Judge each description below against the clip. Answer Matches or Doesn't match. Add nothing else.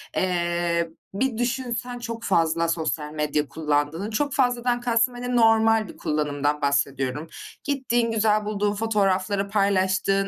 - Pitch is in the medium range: Doesn't match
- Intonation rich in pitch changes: Matches